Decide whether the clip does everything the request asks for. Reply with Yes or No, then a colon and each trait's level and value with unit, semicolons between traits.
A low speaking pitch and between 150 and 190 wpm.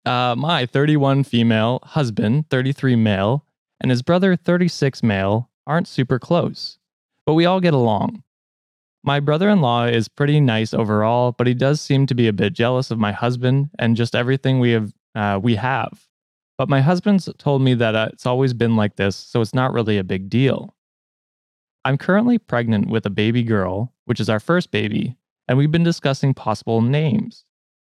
Yes: low, 125 Hz; average, 185 wpm